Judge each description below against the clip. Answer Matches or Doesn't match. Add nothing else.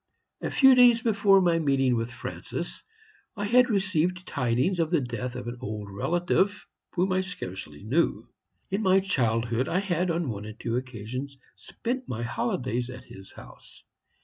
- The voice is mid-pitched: Matches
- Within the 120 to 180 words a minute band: Matches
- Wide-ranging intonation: Matches